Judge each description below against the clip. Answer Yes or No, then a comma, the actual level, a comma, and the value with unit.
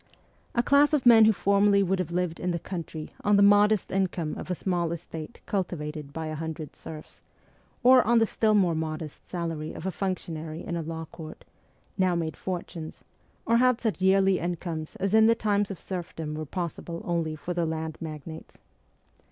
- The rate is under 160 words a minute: No, average, 185 wpm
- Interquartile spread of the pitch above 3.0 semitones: Yes, average, 3.9 semitones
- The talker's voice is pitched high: No, medium, 175 Hz